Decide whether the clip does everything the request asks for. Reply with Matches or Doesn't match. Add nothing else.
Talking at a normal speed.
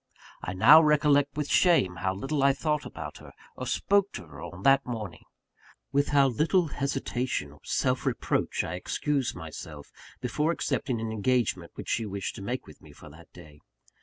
Matches